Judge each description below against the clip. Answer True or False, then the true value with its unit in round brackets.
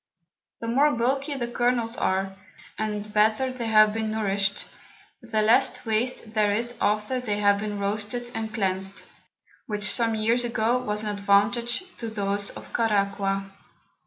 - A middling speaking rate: True (150 wpm)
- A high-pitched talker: True (215 Hz)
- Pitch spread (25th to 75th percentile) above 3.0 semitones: False (2.6 semitones)